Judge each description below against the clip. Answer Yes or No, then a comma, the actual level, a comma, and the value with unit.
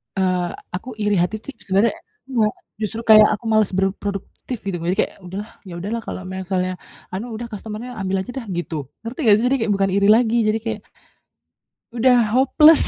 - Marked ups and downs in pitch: No, average, 3.3 semitones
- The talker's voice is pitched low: No, high, 210 Hz